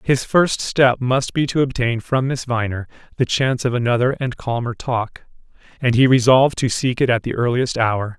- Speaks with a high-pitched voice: No, low, 125 Hz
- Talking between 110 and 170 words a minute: No, average, 200 wpm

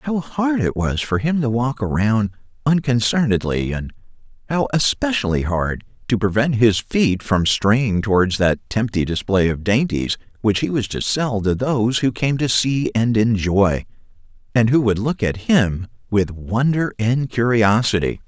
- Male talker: Yes, male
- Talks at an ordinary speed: Yes, average, 160 wpm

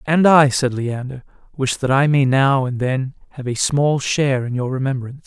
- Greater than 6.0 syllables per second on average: No, 4.9 syllables/s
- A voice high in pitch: No, low, 135 Hz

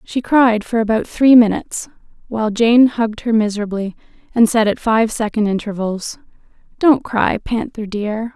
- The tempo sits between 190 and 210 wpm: No, average, 150 wpm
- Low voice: No, high, 225 Hz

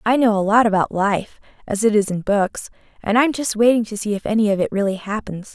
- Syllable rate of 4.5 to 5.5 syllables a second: No, 5.8 syllables/s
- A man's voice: No, female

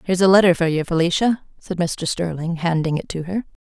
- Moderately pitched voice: Yes, medium, 175 Hz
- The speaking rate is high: Yes, fast, 210 wpm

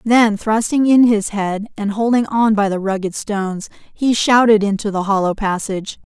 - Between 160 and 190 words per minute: Yes, average, 175 wpm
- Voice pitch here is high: Yes, high, 210 Hz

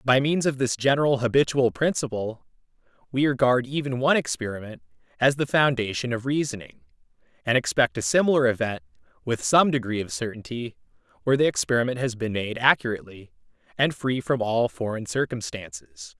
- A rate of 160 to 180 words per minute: No, average, 150 wpm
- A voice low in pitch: Yes, low, 120 Hz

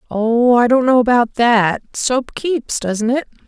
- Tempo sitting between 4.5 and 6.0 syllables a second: No, 3.6 syllables/s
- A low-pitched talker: No, high, 240 Hz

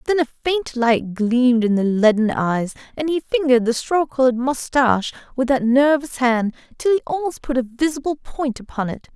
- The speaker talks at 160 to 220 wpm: Yes, average, 190 wpm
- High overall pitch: Yes, very high, 255 Hz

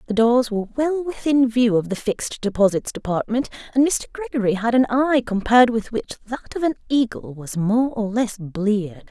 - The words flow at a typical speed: Yes, average, 190 wpm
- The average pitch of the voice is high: Yes, high, 230 Hz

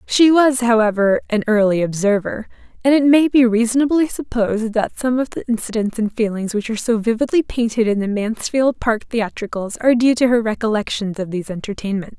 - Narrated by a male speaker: No, female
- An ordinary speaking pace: Yes, average, 180 wpm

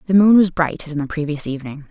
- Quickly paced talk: Yes, fast, 285 wpm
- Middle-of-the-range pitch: Yes, medium, 160 Hz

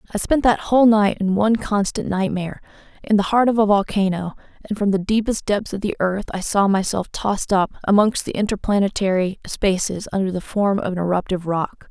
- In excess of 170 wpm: Yes, average, 195 wpm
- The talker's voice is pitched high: Yes, high, 200 Hz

